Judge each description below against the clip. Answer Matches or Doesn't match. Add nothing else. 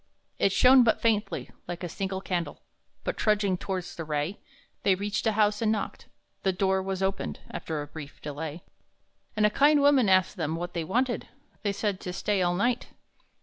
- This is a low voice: Doesn't match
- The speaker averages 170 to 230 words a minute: Matches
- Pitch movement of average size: Matches